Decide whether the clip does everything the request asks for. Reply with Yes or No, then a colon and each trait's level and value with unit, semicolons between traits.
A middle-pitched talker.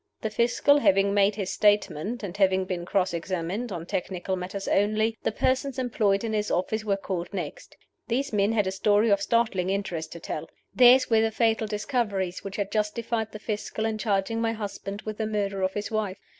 No: high, 205 Hz